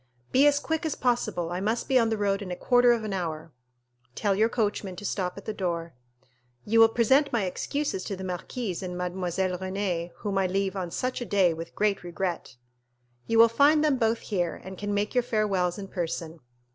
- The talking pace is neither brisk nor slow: No, fast, 210 wpm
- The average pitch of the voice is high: Yes, high, 200 Hz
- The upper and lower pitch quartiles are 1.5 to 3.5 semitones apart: No, average, 4.1 semitones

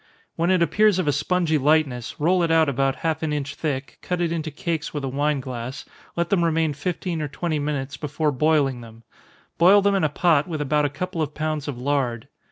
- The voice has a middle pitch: Yes, medium, 155 Hz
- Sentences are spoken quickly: Yes, fast, 220 wpm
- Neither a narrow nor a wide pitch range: Yes, average, 3.2 semitones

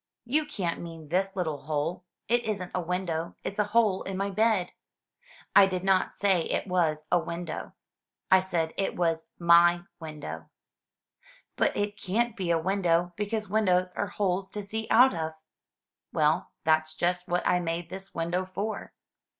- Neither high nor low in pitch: Yes, medium, 180 Hz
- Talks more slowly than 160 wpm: No, average, 170 wpm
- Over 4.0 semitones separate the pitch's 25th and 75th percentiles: No, average, 3.0 semitones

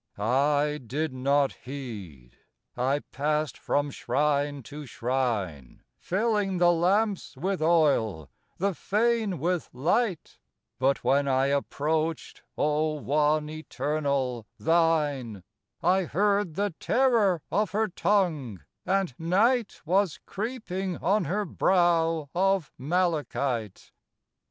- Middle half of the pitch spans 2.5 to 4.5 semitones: No, wide, 5.4 semitones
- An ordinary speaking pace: No, slow, 105 wpm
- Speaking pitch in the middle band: Yes, medium, 155 Hz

